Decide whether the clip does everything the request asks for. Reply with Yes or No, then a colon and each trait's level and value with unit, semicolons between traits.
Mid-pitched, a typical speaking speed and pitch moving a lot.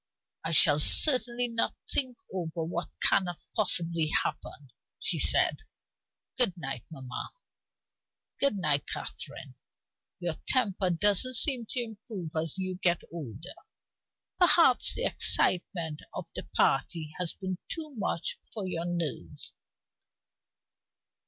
No: medium, 180 Hz; slow, 115 wpm; wide, 5.8 semitones